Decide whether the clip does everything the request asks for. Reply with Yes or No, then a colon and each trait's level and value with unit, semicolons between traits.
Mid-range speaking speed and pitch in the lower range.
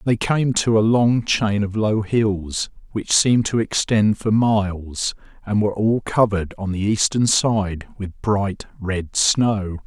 Yes: average, 165 wpm; low, 105 Hz